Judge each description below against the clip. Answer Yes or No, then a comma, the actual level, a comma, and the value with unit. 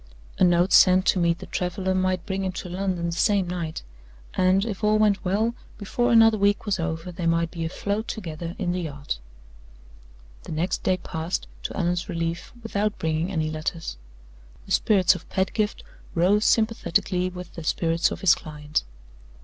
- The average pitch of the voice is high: No, medium, 180 Hz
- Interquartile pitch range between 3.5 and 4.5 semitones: No, average, 3.1 semitones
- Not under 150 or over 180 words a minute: Yes, average, 175 wpm